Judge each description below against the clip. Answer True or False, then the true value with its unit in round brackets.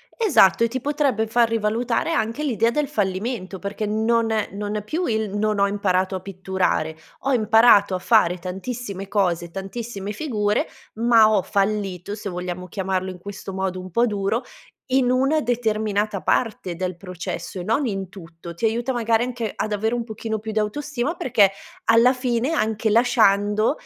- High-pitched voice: True (215 Hz)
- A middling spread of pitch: True (3.5 semitones)